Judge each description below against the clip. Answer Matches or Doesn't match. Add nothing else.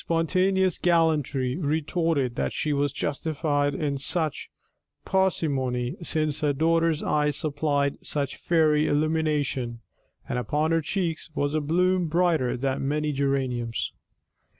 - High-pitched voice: Doesn't match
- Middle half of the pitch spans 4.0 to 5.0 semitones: Doesn't match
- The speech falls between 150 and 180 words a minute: Doesn't match